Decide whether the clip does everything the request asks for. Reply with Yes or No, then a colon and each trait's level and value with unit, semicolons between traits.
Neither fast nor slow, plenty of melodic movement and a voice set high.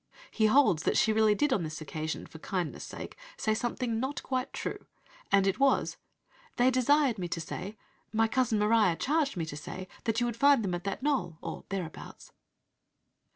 Yes: average, 190 wpm; wide, 5.9 semitones; high, 220 Hz